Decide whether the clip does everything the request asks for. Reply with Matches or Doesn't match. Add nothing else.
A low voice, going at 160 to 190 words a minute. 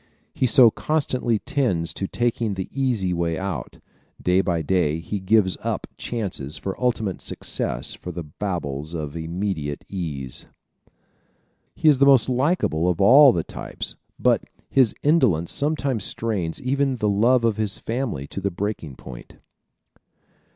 Doesn't match